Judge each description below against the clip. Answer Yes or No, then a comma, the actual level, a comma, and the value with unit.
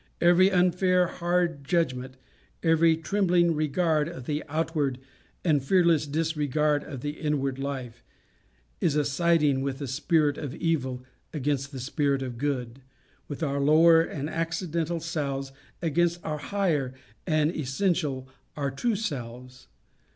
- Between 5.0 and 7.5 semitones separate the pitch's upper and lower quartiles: No, average, 3.5 semitones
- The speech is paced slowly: Yes, slow, 130 wpm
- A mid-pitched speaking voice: Yes, medium, 150 Hz